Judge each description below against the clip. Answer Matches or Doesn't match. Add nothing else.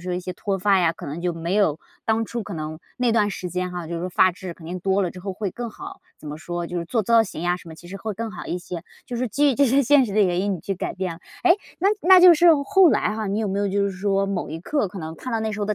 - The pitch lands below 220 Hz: Matches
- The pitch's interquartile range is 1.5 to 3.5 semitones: Doesn't match